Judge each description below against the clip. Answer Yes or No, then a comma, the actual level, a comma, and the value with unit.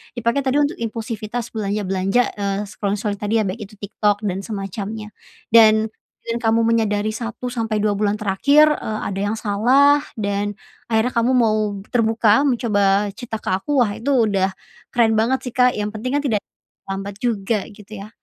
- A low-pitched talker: No, high, 215 Hz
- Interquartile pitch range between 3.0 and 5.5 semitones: No, narrow, 2.4 semitones